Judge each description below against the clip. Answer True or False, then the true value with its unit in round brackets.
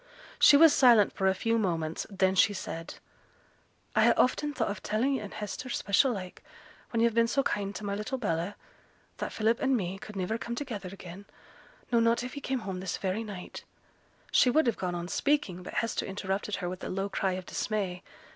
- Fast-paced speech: True (210 wpm)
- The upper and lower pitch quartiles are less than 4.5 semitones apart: True (3.9 semitones)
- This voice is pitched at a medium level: False (205 Hz)